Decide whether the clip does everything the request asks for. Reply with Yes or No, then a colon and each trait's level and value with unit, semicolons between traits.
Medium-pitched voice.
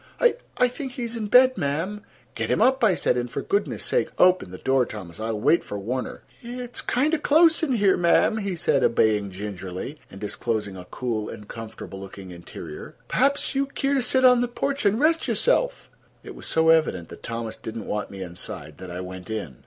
Yes: medium, 145 Hz